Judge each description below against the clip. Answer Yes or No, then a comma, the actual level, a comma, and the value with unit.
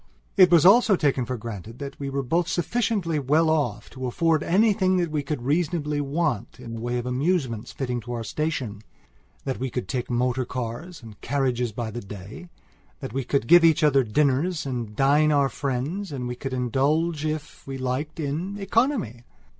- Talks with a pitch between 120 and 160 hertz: Yes, medium, 140 Hz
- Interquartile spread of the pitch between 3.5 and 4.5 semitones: No, average, 4.9 semitones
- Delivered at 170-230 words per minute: Yes, average, 185 wpm